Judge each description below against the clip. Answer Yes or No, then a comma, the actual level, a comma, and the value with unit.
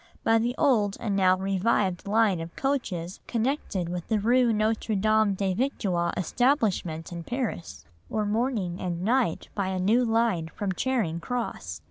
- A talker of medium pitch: No, high, 205 Hz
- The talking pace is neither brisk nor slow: Yes, average, 155 wpm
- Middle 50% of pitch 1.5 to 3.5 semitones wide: No, average, 4.3 semitones